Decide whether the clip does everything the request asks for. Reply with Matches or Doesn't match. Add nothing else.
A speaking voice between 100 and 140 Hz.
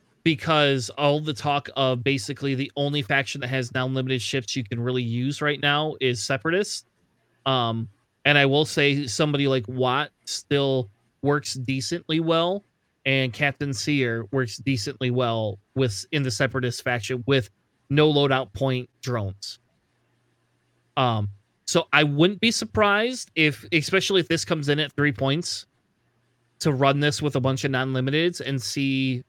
Matches